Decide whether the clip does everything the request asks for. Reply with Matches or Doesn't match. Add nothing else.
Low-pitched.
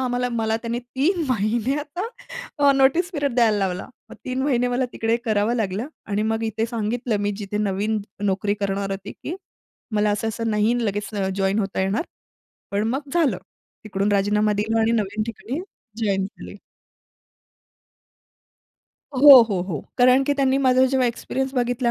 Doesn't match